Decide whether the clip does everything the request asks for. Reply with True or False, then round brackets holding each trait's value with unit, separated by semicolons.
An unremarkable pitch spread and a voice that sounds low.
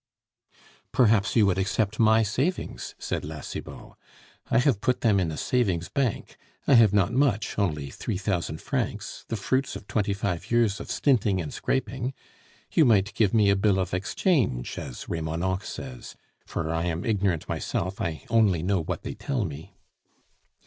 True (4.5 semitones; 100 Hz)